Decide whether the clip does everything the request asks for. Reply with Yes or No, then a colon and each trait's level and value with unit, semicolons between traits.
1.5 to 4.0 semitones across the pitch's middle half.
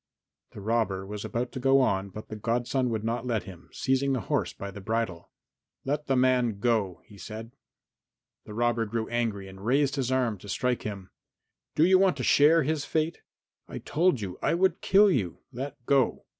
No: average, 4.4 semitones